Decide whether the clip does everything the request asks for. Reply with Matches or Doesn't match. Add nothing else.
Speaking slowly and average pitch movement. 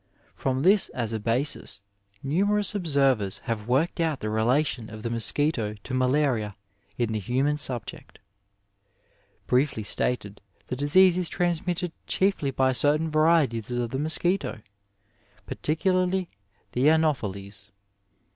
Doesn't match